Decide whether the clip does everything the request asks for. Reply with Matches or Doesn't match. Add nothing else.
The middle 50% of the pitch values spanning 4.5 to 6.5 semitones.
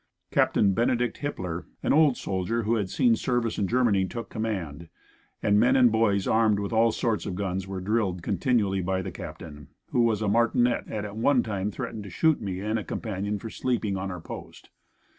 Doesn't match